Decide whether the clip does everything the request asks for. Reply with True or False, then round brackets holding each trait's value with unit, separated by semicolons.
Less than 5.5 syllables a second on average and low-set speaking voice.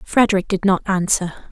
False (5.2 syllables/s; 190 Hz)